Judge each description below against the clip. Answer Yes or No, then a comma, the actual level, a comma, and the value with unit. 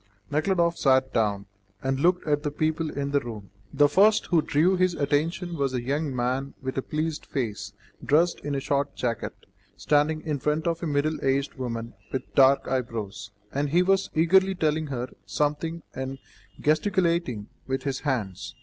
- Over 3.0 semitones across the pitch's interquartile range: Yes, average, 3.6 semitones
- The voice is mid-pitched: Yes, medium, 145 Hz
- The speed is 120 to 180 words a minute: Yes, average, 170 wpm